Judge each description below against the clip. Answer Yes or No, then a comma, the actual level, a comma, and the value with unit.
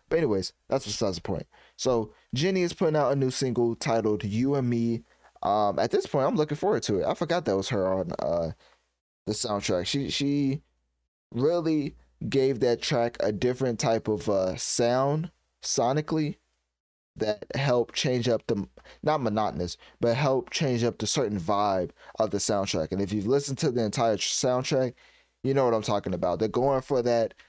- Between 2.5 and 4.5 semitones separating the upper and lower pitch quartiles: No, average, 4.9 semitones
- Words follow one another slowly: No, average, 185 wpm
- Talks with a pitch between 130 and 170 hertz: No, low, 120 Hz